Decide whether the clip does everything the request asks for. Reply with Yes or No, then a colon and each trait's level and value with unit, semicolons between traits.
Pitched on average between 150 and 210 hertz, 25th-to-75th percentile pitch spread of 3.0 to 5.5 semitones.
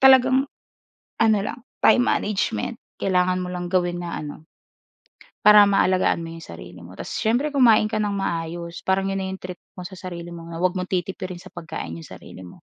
Yes: medium, 185 Hz; average, 3.6 semitones